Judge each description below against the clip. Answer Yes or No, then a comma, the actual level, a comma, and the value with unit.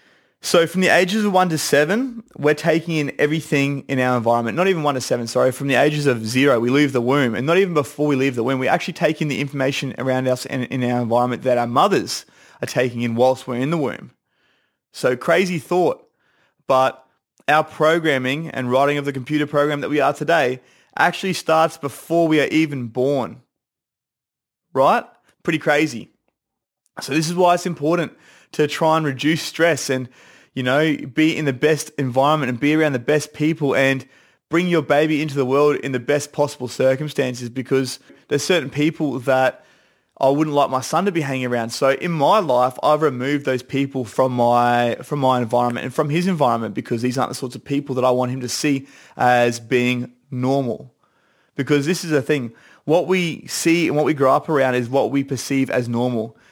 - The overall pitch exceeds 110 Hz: Yes, medium, 140 Hz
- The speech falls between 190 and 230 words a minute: Yes, fast, 205 wpm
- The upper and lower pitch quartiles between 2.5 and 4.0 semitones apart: Yes, average, 3.4 semitones